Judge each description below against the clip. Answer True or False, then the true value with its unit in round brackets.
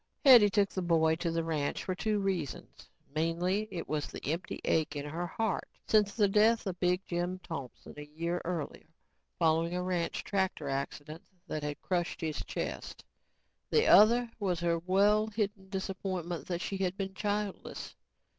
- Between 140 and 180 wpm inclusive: True (165 wpm)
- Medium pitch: True (180 Hz)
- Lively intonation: False (3.4 semitones)